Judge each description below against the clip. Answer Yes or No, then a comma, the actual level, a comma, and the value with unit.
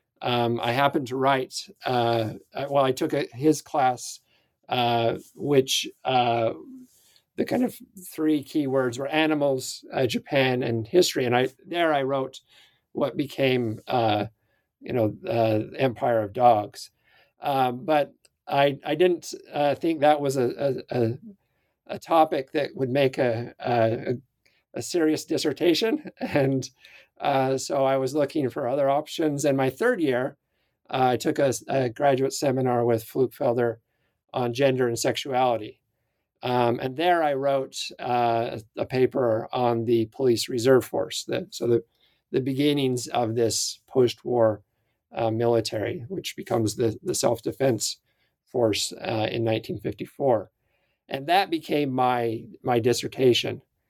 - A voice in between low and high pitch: No, low, 130 Hz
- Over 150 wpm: No, average, 140 wpm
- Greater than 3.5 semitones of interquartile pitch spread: No, average, 3.2 semitones